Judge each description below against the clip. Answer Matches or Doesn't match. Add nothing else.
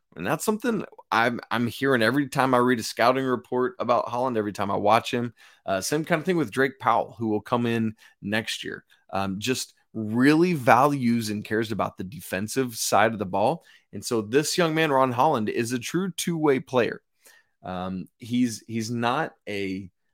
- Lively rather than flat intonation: Doesn't match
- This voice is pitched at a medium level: Doesn't match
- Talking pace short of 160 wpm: Doesn't match